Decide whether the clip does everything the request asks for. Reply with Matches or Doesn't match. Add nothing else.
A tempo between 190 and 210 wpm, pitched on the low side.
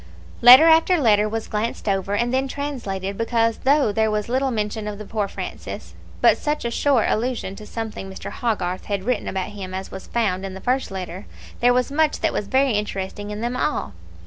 Doesn't match